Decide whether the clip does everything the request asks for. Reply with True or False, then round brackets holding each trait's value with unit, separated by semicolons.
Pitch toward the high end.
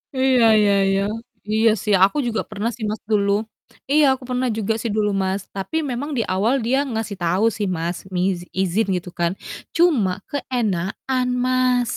True (215 Hz)